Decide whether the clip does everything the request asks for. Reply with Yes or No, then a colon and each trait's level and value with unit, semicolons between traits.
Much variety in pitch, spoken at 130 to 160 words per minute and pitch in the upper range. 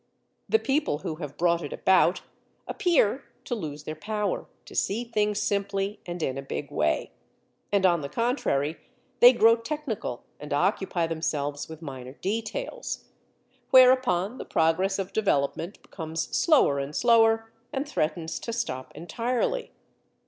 Yes: wide, 6.8 semitones; average, 140 wpm; high, 195 Hz